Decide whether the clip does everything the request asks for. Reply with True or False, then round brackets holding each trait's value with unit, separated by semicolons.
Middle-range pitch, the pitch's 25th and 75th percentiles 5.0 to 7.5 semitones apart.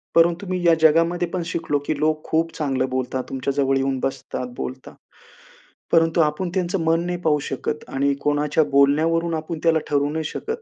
False (155 Hz; 3.0 semitones)